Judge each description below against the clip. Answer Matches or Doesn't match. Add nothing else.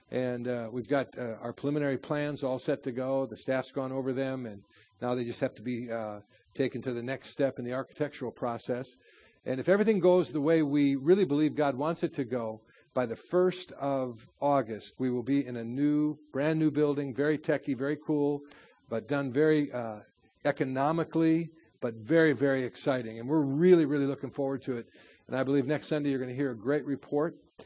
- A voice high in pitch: Doesn't match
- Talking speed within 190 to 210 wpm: Matches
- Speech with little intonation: Doesn't match